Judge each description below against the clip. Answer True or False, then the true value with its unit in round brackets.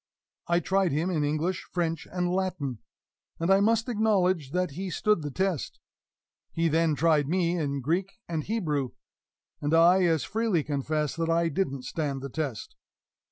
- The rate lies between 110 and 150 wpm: False (160 wpm)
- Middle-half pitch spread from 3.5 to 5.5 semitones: True (3.9 semitones)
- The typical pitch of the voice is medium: True (165 Hz)